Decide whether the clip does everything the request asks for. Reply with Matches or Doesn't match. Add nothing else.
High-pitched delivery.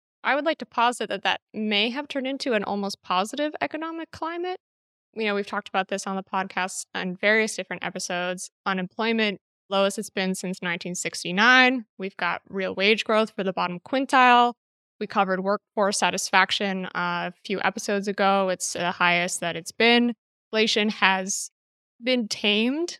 Matches